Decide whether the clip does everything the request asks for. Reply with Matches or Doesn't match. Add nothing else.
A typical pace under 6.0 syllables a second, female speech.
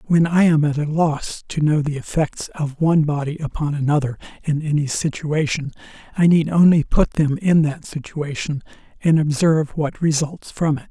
Doesn't match